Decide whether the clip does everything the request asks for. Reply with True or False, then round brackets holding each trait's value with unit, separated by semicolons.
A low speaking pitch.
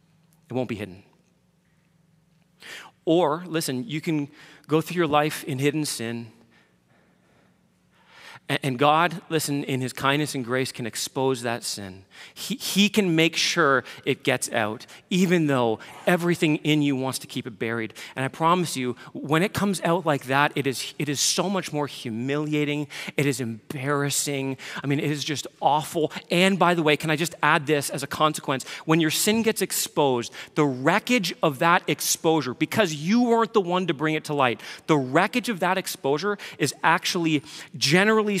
False (155 Hz)